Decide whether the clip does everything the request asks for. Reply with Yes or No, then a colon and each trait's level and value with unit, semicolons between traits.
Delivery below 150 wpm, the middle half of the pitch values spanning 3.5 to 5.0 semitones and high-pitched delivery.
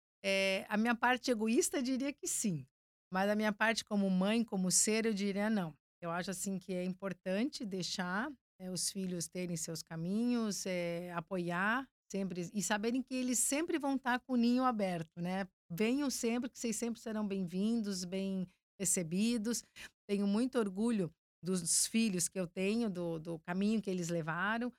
No: average, 175 wpm; average, 4.1 semitones; high, 200 Hz